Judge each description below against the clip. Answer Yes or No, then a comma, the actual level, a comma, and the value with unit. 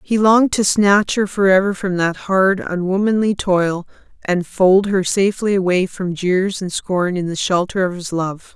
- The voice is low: No, high, 190 Hz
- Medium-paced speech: Yes, average, 180 wpm